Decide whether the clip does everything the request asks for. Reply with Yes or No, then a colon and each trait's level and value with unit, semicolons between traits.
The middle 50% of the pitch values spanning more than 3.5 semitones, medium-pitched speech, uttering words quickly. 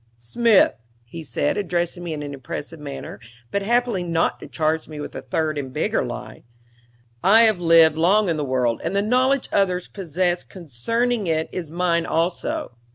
No: average, 4.4 semitones; medium, 170 Hz; average, 175 wpm